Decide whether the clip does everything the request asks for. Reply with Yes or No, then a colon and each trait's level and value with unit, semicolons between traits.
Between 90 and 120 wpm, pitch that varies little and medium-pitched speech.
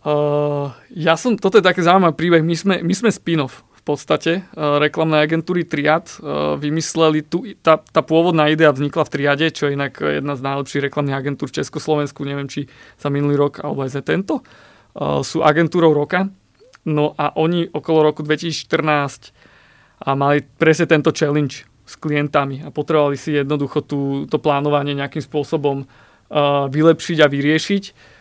No: fast, 165 wpm; narrow, 2.2 semitones; medium, 150 Hz